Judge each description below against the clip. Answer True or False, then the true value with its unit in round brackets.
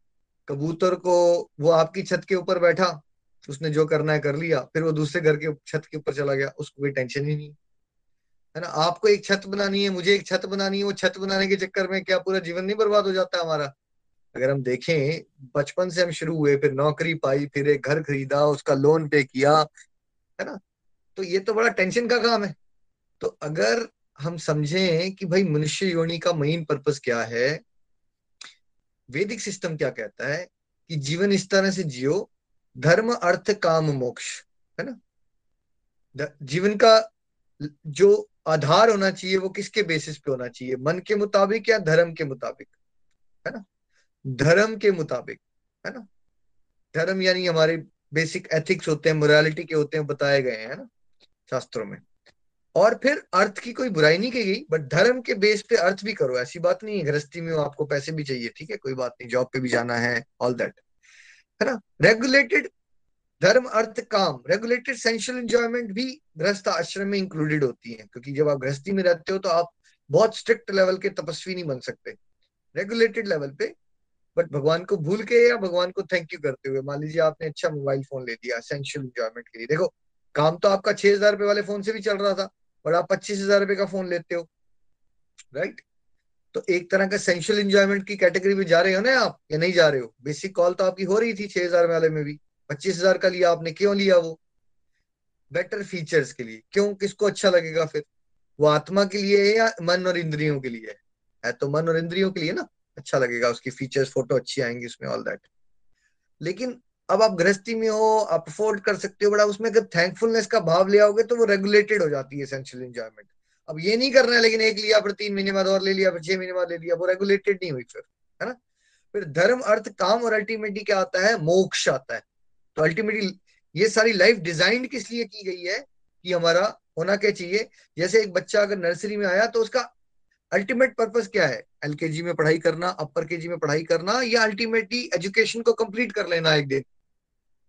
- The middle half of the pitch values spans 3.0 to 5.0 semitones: False (5.4 semitones)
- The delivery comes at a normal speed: False (200 wpm)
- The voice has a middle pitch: True (180 Hz)